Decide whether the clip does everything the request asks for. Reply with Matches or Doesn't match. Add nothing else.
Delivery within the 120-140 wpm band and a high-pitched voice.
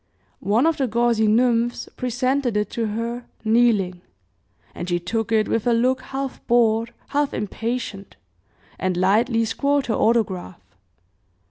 Matches